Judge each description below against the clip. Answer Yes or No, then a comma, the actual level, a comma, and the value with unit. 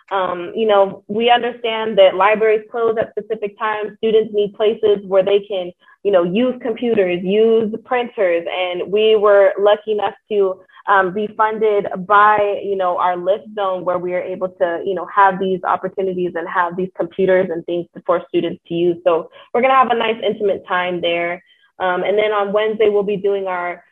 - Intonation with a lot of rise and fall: No, average, 2.9 semitones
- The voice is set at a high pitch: Yes, high, 200 Hz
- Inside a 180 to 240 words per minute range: Yes, average, 190 wpm